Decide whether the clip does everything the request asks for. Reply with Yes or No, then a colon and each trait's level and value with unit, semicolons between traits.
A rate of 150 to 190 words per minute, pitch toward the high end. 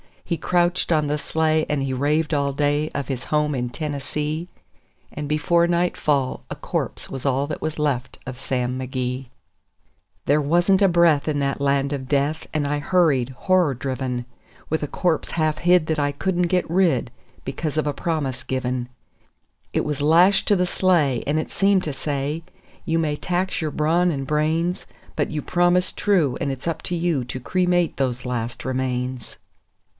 No: average, 180 wpm; medium, 150 Hz